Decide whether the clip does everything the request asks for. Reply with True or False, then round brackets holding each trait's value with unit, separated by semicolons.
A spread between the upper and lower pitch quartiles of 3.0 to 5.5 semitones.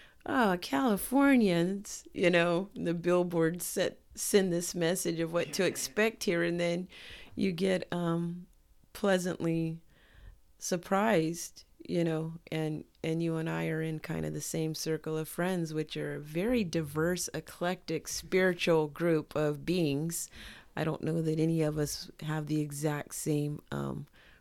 False (2.5 semitones)